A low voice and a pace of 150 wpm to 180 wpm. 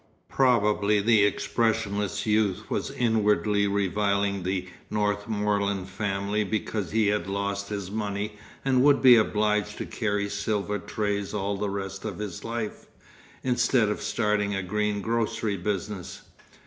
No: low, 105 Hz; slow, 135 wpm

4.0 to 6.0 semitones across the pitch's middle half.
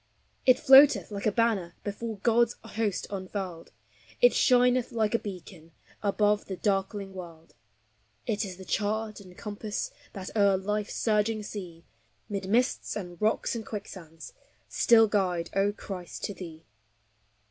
No: average, 2.9 semitones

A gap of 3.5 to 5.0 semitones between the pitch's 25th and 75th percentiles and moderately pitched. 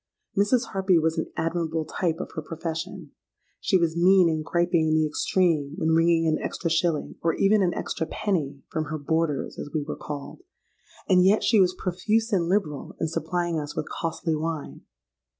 No: narrow, 2.6 semitones; medium, 165 Hz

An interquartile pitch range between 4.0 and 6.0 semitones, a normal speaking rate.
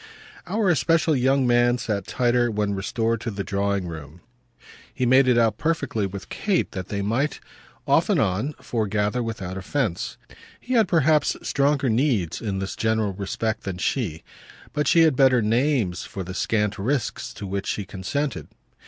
Yes: wide, 5.5 semitones; average, 165 wpm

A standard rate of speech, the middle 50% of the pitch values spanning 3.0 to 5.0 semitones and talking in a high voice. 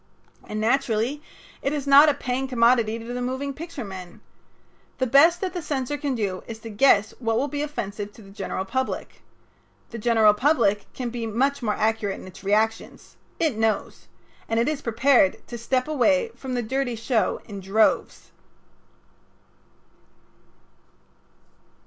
Yes: average, 155 wpm; average, 4.1 semitones; high, 240 Hz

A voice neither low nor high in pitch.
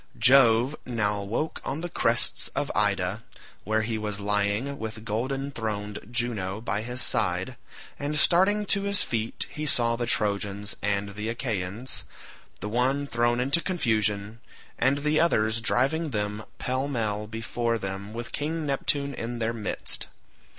No: low, 115 Hz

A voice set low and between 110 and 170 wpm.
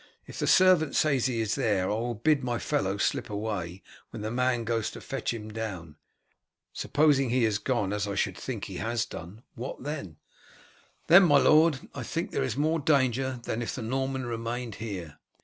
No: low, 120 Hz; average, 195 wpm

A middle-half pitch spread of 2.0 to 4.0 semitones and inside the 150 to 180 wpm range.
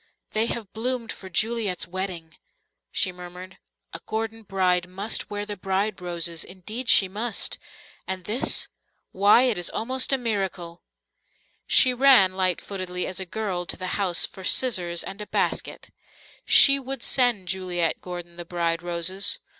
Yes: average, 3.7 semitones; average, 155 wpm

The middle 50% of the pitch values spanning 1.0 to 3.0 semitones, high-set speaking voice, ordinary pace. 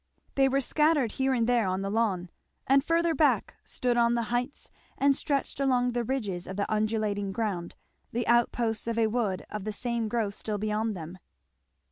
No: average, 3.4 semitones; high, 230 Hz; average, 185 wpm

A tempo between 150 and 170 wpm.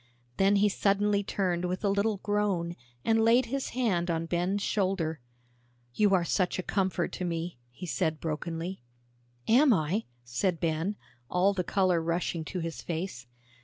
Yes: average, 160 wpm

